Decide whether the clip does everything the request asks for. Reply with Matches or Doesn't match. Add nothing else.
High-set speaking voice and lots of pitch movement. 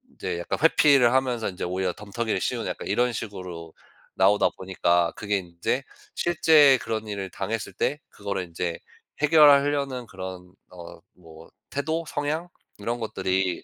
Doesn't match